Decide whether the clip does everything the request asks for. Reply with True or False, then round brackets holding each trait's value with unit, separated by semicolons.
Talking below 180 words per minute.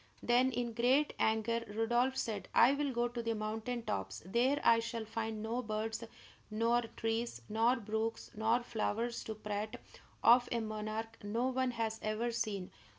True (160 wpm)